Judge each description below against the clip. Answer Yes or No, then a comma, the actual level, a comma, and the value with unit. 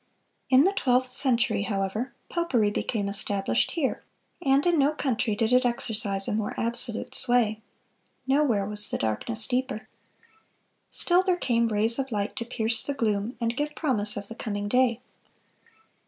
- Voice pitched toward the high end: Yes, high, 235 Hz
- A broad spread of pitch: No, average, 4.0 semitones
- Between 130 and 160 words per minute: Yes, average, 155 wpm